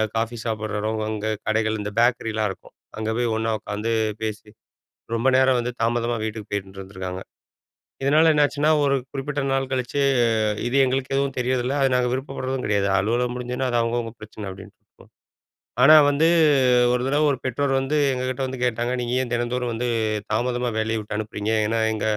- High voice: No, low, 120 Hz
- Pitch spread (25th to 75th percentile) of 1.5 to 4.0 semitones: Yes, average, 3.0 semitones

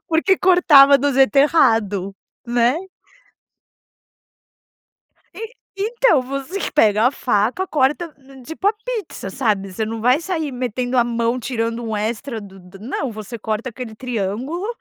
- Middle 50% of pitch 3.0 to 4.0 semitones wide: No, average, 5.3 semitones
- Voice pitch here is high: Yes, very high, 250 Hz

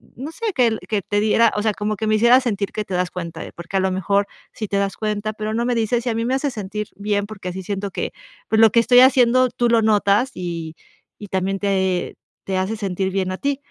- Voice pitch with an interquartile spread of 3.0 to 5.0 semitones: Yes, average, 3.3 semitones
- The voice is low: No, high, 210 Hz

